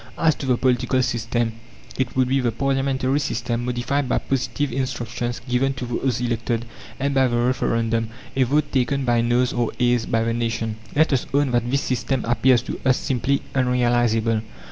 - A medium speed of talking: Yes, average, 180 wpm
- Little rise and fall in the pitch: Yes, narrow, 2.1 semitones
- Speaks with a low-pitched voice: Yes, low, 125 Hz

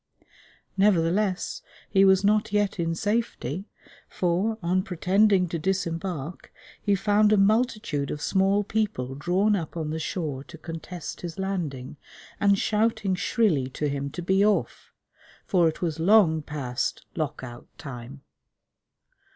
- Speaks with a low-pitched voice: No, medium, 180 Hz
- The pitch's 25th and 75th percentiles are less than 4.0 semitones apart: No, average, 4.7 semitones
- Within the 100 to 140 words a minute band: Yes, slow, 135 wpm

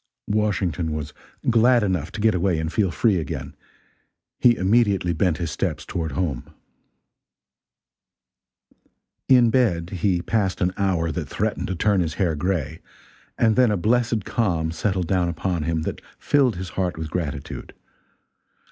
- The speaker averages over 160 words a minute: No, average, 145 wpm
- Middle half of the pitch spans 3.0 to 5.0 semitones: Yes, average, 4.5 semitones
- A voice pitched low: Yes, very low, 90 Hz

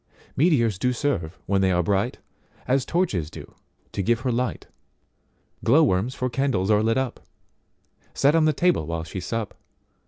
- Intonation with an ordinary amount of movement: No, wide, 6.0 semitones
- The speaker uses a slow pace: No, average, 150 wpm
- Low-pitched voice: Yes, low, 115 Hz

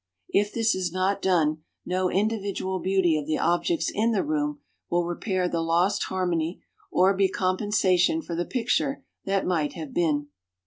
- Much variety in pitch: No, average, 2.9 semitones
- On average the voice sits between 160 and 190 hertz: Yes, medium, 185 Hz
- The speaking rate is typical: Yes, average, 165 wpm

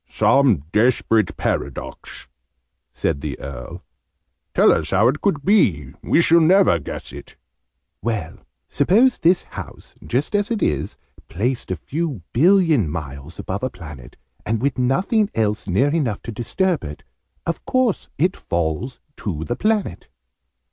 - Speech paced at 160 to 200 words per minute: No, average, 140 wpm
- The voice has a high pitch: No, low, 125 Hz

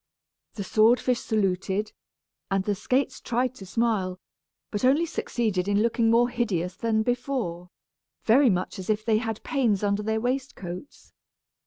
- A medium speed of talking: Yes, average, 150 wpm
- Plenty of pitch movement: No, average, 3.8 semitones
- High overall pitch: Yes, high, 220 Hz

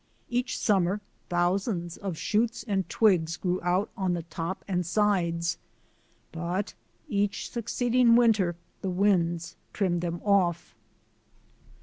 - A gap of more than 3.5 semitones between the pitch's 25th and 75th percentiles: No, average, 3.2 semitones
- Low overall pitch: No, medium, 185 Hz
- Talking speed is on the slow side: Yes, slow, 115 wpm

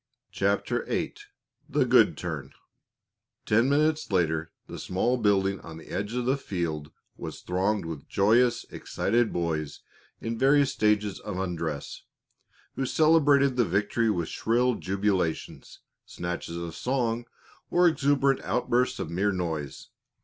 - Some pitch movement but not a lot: No, wide, 6.3 semitones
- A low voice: Yes, low, 105 Hz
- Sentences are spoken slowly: Yes, slow, 130 wpm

